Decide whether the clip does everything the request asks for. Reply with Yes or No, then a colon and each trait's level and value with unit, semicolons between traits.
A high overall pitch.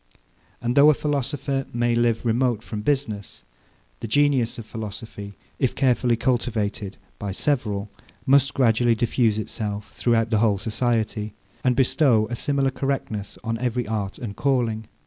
No: low, 115 Hz